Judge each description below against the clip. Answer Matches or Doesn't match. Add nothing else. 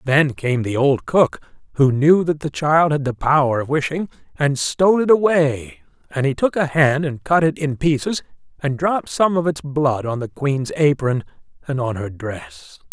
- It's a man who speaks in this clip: Matches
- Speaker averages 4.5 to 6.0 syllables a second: Matches